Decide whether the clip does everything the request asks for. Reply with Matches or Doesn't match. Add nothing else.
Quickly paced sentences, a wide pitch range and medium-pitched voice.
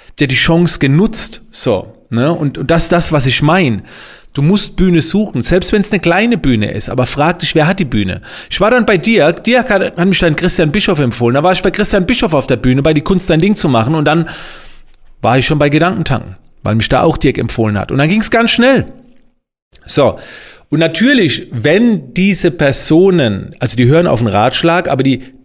Matches